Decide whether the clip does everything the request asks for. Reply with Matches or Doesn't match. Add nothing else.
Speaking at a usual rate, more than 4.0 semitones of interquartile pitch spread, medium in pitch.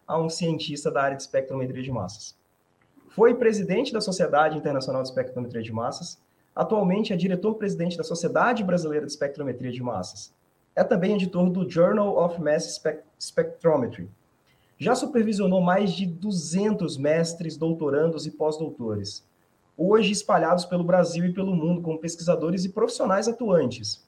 Matches